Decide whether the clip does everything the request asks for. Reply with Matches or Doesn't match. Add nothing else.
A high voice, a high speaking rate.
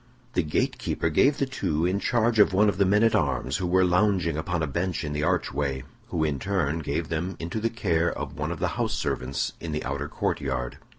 Doesn't match